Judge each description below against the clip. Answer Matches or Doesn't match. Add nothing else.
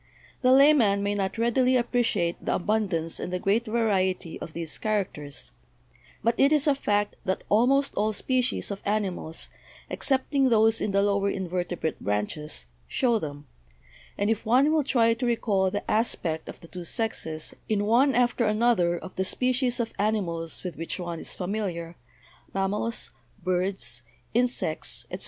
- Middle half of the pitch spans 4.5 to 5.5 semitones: Matches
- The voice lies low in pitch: Doesn't match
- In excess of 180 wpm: Doesn't match